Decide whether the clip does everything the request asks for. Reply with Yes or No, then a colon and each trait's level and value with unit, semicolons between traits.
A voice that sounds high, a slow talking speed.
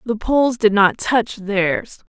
No: high, 215 Hz; average, 170 wpm